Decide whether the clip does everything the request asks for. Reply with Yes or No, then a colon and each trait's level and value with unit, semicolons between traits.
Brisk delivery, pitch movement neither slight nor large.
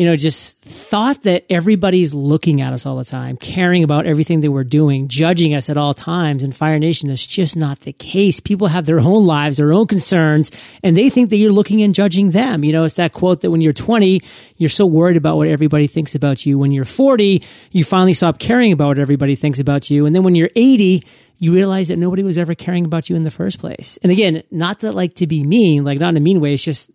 Yes: fast, 250 wpm; average, 4.0 semitones